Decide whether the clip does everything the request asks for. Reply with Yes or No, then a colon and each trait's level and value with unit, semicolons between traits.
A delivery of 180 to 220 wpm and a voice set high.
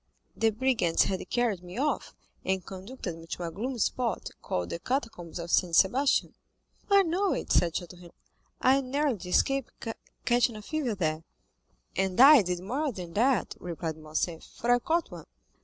No: average, 170 wpm; high, 210 Hz